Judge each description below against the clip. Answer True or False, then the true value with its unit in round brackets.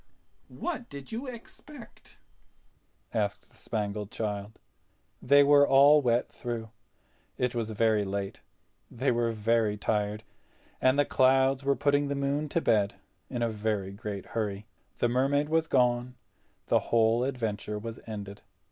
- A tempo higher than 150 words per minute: False (140 wpm)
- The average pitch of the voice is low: True (120 Hz)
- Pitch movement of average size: True (4.7 semitones)